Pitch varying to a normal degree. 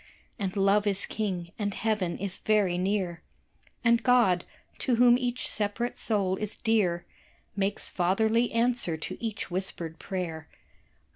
Yes: average, 3.6 semitones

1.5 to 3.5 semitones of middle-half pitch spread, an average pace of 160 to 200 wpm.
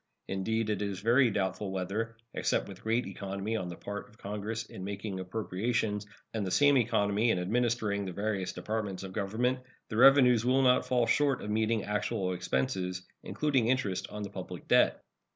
Yes: average, 3.1 semitones; average, 175 wpm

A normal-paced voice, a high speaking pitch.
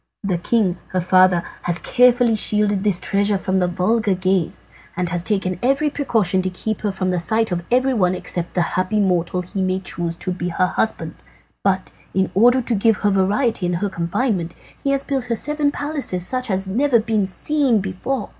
Yes: average, 195 wpm; high, 195 Hz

